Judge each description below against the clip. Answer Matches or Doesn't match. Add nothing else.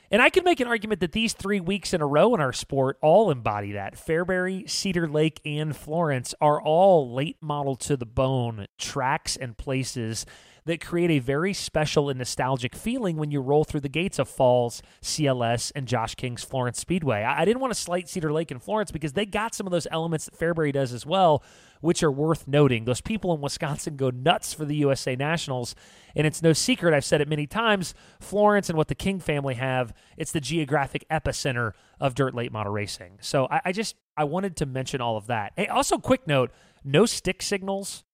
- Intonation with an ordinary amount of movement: Matches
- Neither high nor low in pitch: Matches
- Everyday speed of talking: Doesn't match